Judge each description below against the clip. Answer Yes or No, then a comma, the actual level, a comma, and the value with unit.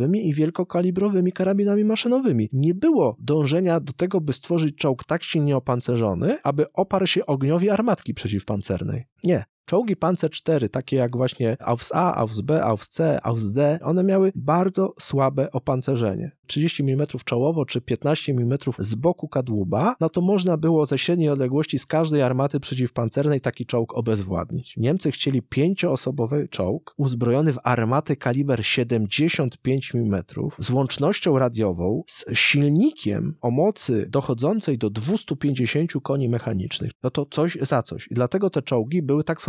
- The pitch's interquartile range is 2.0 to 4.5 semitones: No, average, 4.9 semitones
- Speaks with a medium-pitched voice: Yes, medium, 145 Hz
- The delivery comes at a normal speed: Yes, average, 140 wpm